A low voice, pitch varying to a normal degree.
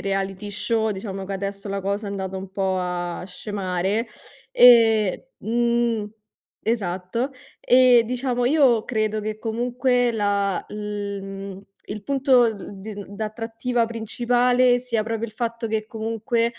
No: high, 220 Hz; average, 3.2 semitones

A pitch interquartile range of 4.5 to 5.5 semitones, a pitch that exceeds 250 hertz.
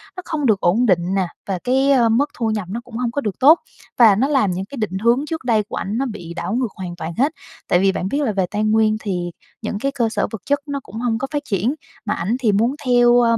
No: average, 4.8 semitones; high, 225 Hz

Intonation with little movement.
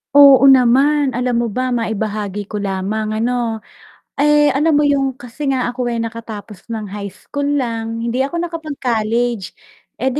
No: average, 3.7 semitones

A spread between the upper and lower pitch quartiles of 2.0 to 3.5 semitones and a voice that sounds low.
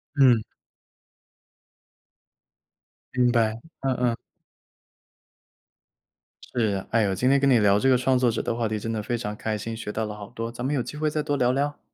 Yes: average, 3.1 semitones; low, 120 Hz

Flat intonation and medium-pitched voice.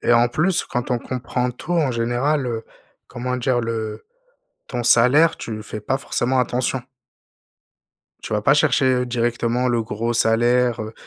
No: narrow, 1.7 semitones; low, 120 Hz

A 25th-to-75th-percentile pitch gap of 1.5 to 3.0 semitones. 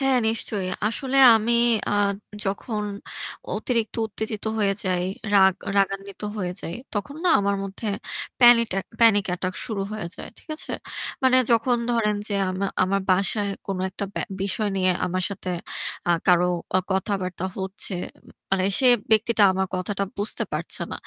Yes: average, 2.7 semitones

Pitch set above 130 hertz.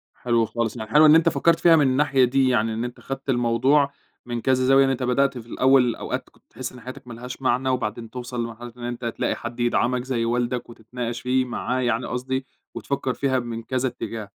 No: low, 125 Hz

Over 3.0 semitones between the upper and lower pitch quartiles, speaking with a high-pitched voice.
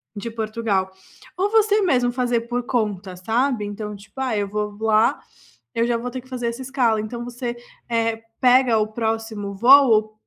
No: narrow, 2.6 semitones; high, 230 Hz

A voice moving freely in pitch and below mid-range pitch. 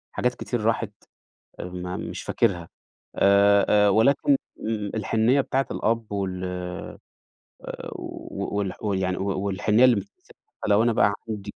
No: average, 3.0 semitones; low, 100 Hz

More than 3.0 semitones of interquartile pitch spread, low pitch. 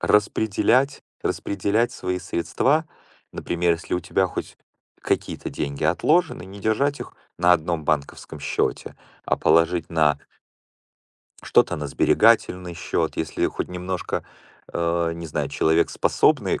Yes: average, 3.6 semitones; very low, 90 Hz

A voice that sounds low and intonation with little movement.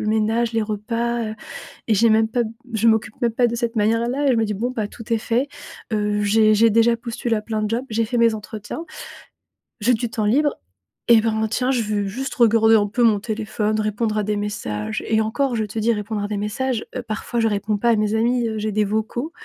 No: high, 220 Hz; narrow, 1.8 semitones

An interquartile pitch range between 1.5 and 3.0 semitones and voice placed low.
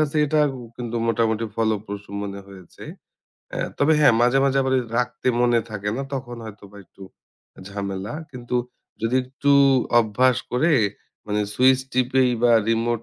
No: average, 3.6 semitones; low, 120 Hz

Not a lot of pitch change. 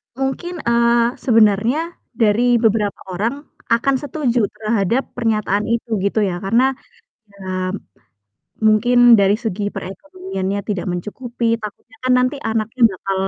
No: average, 3.1 semitones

